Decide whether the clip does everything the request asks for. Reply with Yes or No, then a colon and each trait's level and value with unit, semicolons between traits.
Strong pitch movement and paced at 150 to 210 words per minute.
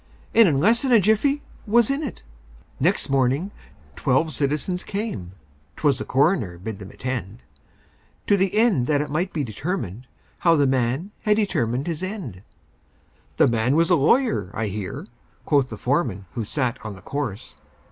Yes: wide, 8.6 semitones; average, 165 wpm